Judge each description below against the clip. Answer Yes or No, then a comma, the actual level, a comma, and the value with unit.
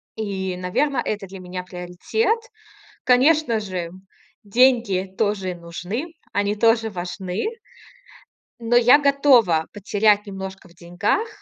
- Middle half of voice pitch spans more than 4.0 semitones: Yes, average, 4.8 semitones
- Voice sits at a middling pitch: No, high, 205 Hz